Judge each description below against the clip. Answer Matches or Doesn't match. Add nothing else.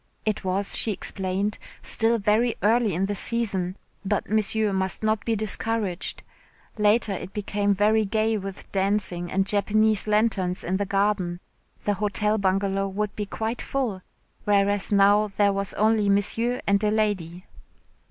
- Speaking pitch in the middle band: Doesn't match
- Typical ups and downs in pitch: Doesn't match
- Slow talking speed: Doesn't match